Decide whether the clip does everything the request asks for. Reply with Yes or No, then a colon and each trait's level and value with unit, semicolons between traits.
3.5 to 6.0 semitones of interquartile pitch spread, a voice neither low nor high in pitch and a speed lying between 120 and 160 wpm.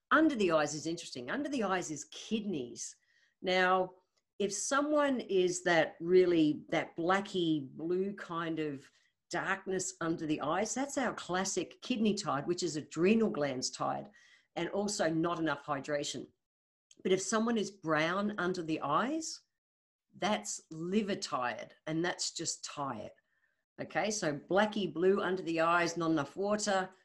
Yes: average, 3.9 semitones; medium, 180 Hz; average, 145 wpm